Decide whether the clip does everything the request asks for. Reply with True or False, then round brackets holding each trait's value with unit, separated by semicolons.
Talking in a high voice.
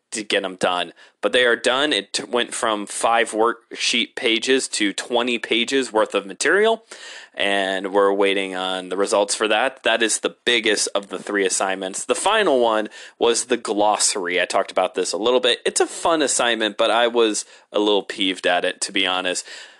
False (115 Hz)